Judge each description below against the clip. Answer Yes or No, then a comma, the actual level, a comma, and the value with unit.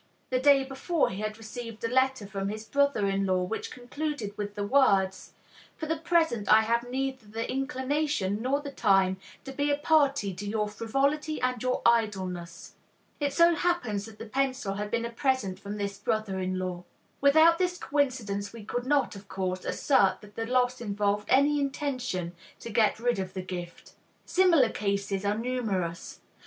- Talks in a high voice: Yes, high, 230 Hz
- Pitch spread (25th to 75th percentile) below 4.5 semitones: No, average, 5.3 semitones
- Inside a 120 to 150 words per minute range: No, average, 180 wpm